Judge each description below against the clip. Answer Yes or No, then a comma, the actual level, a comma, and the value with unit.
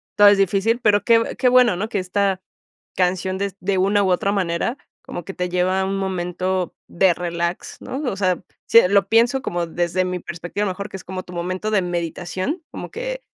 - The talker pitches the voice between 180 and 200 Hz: Yes, high, 190 Hz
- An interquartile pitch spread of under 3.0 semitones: Yes, narrow, 2.4 semitones